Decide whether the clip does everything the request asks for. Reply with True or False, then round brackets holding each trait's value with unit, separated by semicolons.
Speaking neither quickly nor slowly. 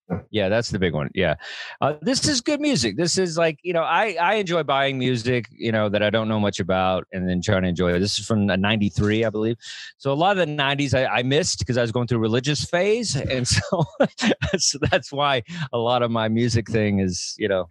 False (245 wpm)